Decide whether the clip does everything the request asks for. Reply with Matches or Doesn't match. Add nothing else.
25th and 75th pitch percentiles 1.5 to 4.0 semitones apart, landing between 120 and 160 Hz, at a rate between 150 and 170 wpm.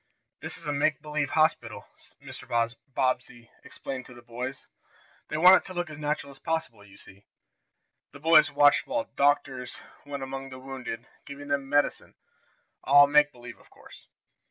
Matches